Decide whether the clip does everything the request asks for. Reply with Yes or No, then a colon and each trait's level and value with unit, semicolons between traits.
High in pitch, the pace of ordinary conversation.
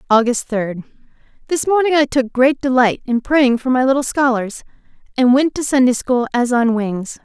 Yes: very high, 255 Hz; average, 175 wpm